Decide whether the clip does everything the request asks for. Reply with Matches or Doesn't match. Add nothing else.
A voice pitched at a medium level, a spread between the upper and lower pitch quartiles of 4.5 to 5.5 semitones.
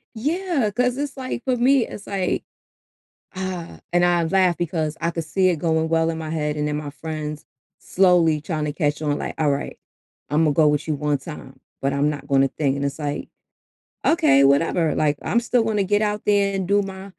Matches